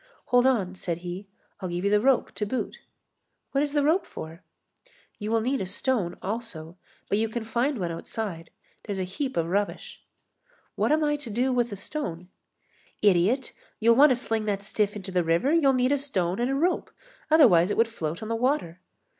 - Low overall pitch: No, high, 220 Hz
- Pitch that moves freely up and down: Yes, wide, 6.2 semitones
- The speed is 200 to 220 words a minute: Yes, fast, 205 wpm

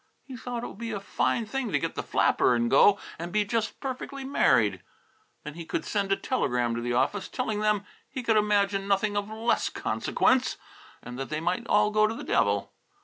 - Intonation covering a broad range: Yes, wide, 5.9 semitones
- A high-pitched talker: Yes, high, 205 Hz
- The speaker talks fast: Yes, fast, 210 wpm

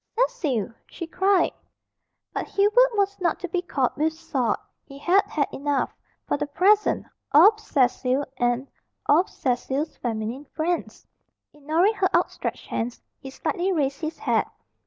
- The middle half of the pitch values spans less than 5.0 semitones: No, wide, 5.6 semitones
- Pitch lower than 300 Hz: No, very high, 310 Hz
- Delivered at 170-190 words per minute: No, average, 140 wpm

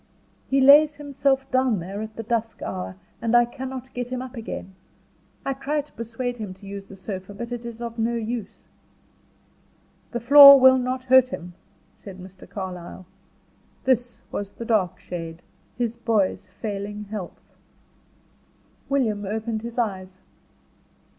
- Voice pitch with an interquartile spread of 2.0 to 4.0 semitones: No, average, 4.4 semitones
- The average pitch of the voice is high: Yes, high, 230 Hz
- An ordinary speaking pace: Yes, average, 150 wpm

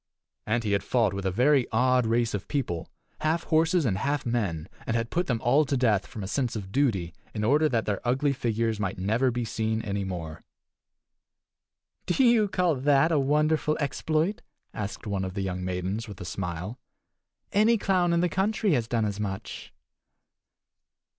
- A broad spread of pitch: Yes, wide, 6.8 semitones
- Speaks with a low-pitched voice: Yes, low, 120 Hz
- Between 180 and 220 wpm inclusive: Yes, average, 185 wpm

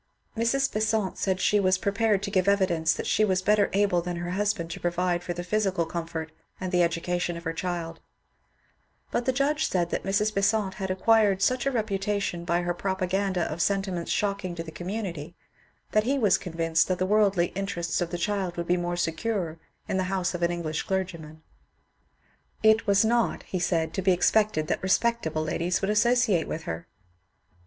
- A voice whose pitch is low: No, medium, 185 Hz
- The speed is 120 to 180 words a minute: No, average, 190 wpm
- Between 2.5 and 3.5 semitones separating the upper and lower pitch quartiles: Yes, average, 3.2 semitones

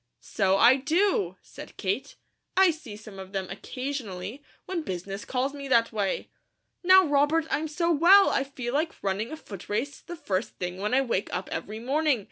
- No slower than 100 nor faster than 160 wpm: No, average, 180 wpm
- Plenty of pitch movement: Yes, wide, 7.5 semitones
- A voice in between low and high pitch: No, very high, 260 Hz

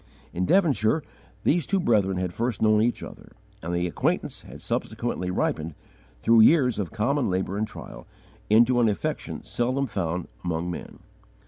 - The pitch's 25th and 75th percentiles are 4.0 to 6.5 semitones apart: Yes, wide, 5.4 semitones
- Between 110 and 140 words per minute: No, average, 155 wpm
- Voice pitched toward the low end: Yes, low, 110 Hz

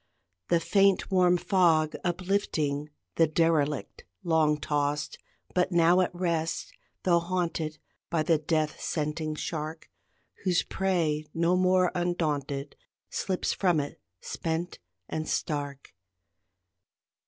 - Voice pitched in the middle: Yes, medium, 165 Hz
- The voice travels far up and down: No, average, 2.8 semitones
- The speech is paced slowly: Yes, slow, 110 wpm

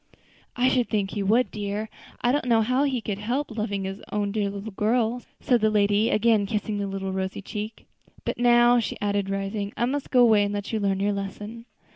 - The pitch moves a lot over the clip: No, average, 2.9 semitones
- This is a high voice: Yes, high, 210 Hz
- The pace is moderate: No, fast, 215 wpm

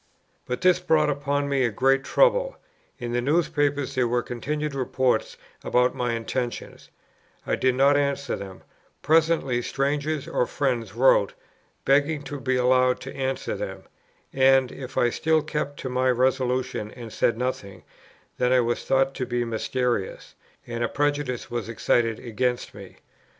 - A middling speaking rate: Yes, average, 155 wpm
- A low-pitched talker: Yes, low, 130 Hz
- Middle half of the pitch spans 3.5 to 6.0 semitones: No, average, 2.8 semitones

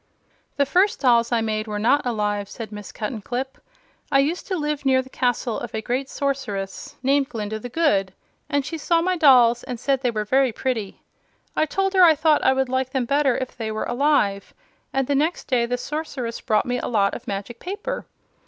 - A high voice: Yes, very high, 255 Hz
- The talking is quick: Yes, fast, 210 wpm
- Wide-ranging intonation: No, average, 4.3 semitones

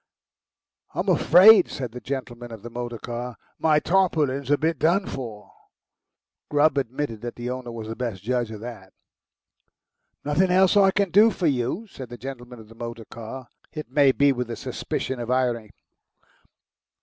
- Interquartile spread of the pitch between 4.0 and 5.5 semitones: Yes, average, 4.4 semitones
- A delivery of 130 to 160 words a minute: No, average, 170 wpm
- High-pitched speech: No, low, 125 Hz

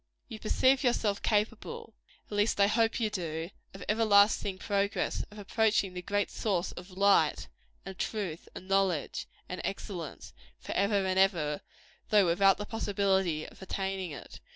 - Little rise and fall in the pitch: Yes, narrow, 2.1 semitones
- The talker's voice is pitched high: Yes, high, 200 Hz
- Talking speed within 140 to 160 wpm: Yes, average, 150 wpm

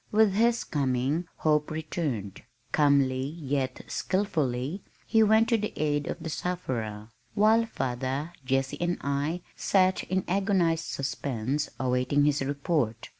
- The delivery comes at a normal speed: No, slow, 125 wpm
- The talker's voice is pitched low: No, medium, 150 Hz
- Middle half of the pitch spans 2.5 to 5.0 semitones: No, wide, 5.5 semitones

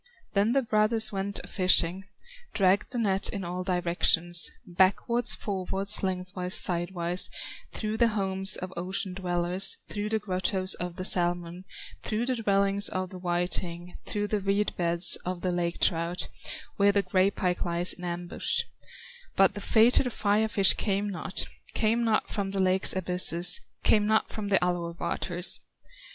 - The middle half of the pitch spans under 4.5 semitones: Yes, narrow, 2.5 semitones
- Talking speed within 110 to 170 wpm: Yes, average, 155 wpm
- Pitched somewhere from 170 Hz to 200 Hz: Yes, high, 190 Hz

